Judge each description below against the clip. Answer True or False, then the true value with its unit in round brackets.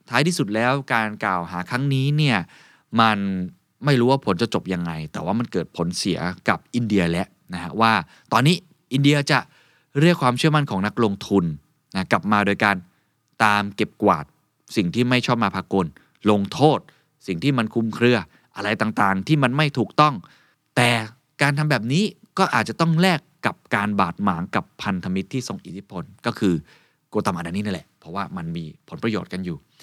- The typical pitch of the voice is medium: False (115 Hz)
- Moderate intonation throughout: False (6.1 semitones)